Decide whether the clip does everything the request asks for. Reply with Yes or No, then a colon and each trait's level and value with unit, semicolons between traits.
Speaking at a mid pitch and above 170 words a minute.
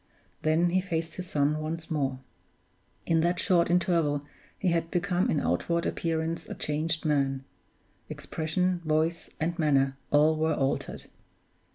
No: medium, 160 Hz; average, 140 wpm